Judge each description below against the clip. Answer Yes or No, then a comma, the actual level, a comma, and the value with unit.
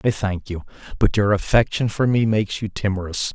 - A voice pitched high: No, low, 105 Hz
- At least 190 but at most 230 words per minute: Yes, average, 200 wpm